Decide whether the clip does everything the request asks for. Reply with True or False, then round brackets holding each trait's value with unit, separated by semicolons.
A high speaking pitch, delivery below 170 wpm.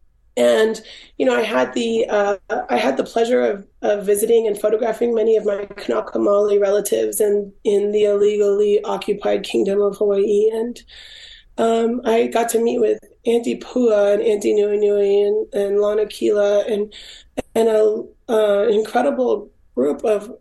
True (210 Hz; 155 wpm)